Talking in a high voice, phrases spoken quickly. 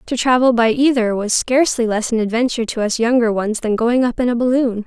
Yes: high, 235 Hz; fast, 235 wpm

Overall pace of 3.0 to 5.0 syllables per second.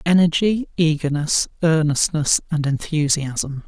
Yes: 4.0 syllables/s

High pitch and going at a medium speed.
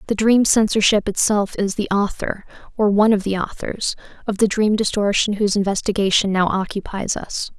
Yes: high, 205 Hz; average, 165 wpm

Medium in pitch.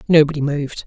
Yes: medium, 150 Hz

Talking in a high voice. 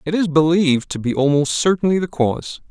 No: medium, 160 Hz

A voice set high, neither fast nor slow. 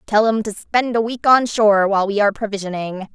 No: high, 215 Hz; fast, 230 wpm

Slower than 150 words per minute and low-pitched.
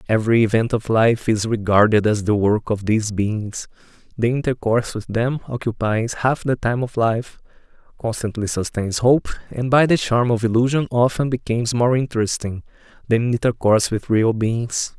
No: average, 160 wpm; low, 115 Hz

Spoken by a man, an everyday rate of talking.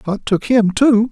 No: male; fast, 215 wpm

